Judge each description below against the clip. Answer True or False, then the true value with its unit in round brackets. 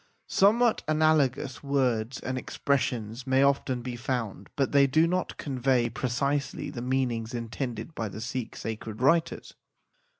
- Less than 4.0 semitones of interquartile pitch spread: True (2.9 semitones)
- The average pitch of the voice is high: False (130 Hz)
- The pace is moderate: True (145 wpm)